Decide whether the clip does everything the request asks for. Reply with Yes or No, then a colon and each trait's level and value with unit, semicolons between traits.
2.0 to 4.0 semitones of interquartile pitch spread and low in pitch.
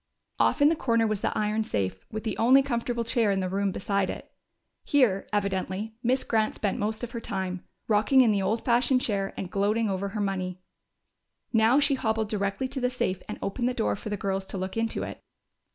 No: average, 3.3 semitones; high, 215 Hz